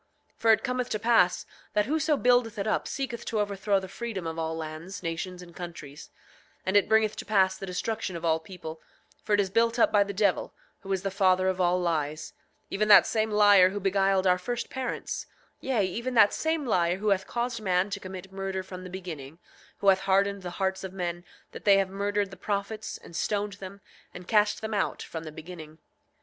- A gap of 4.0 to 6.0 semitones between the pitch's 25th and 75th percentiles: No, average, 2.8 semitones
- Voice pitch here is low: No, high, 195 Hz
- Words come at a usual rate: No, fast, 215 wpm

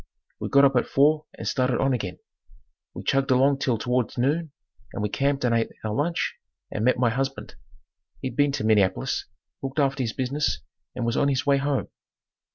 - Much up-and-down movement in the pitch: No, narrow, 2.6 semitones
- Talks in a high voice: No, low, 135 Hz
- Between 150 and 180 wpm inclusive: No, average, 190 wpm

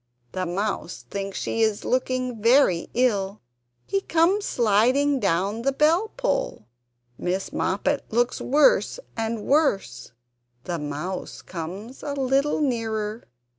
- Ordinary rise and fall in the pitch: No, wide, 6.2 semitones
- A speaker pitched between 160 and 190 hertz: No, high, 230 Hz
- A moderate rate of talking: No, slow, 115 wpm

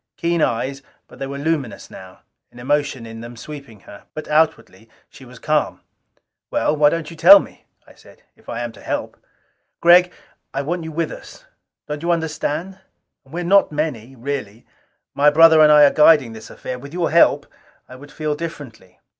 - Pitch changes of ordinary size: Yes, average, 4.1 semitones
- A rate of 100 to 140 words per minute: No, average, 190 wpm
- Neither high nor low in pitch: Yes, medium, 150 Hz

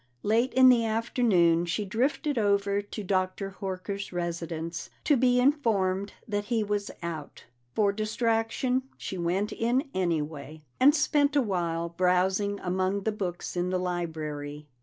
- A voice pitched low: No, high, 200 Hz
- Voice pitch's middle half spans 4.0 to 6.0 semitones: Yes, average, 4.5 semitones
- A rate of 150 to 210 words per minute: No, average, 140 wpm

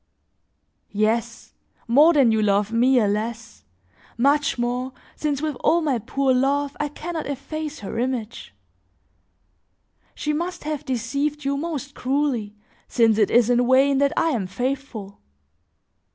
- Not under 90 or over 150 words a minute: Yes, average, 140 wpm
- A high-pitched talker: Yes, very high, 265 Hz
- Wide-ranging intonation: No, average, 4.0 semitones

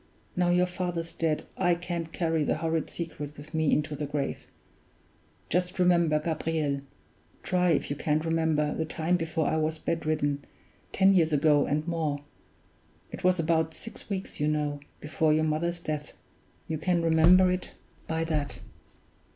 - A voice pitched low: No, medium, 160 Hz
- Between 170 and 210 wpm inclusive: No, average, 160 wpm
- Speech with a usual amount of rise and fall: No, narrow, 2.1 semitones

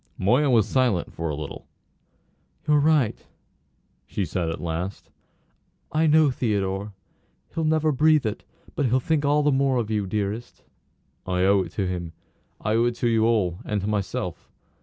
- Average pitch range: No, wide, 6.7 semitones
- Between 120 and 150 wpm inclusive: No, average, 170 wpm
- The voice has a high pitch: No, low, 110 Hz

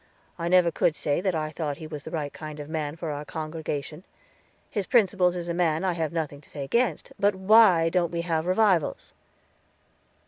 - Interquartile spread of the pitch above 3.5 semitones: No, average, 2.8 semitones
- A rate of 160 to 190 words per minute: No, average, 200 wpm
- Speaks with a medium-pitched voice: Yes, medium, 165 Hz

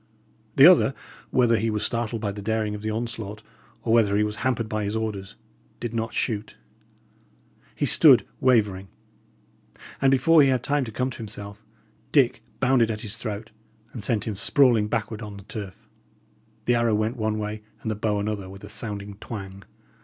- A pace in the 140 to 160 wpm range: No, average, 185 wpm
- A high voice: No, low, 110 Hz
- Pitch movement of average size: No, narrow, 2.2 semitones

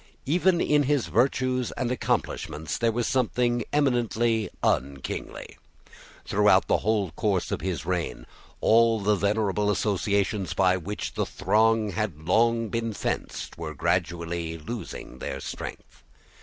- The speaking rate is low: Yes, slow, 130 wpm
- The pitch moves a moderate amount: Yes, average, 4.7 semitones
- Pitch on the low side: Yes, low, 105 Hz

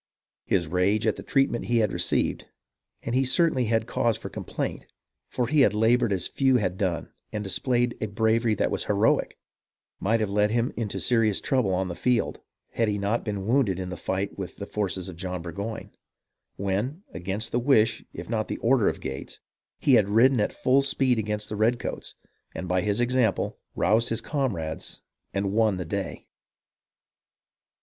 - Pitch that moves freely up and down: No, average, 3.8 semitones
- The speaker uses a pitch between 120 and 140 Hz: No, low, 110 Hz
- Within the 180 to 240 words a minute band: Yes, average, 185 wpm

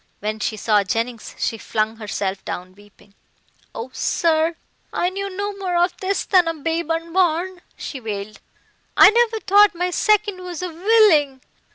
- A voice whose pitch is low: No, very high, 330 Hz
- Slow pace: No, average, 160 wpm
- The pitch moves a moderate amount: No, wide, 9.0 semitones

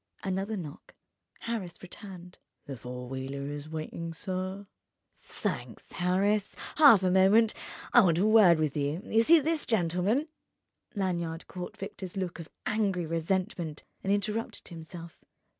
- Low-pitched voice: No, medium, 185 Hz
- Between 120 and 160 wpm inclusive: Yes, slow, 135 wpm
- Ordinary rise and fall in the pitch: Yes, average, 3.9 semitones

